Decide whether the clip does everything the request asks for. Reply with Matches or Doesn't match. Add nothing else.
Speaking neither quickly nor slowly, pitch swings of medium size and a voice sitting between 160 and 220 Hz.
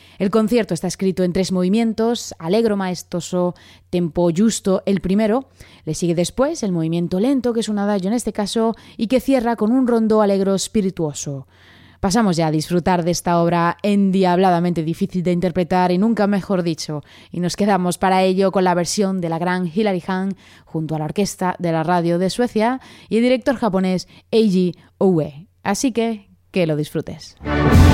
Matches